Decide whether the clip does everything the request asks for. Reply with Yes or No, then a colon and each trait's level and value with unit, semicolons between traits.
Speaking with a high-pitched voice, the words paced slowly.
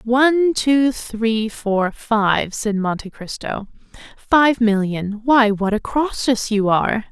Yes: high, 225 Hz; slow, 125 wpm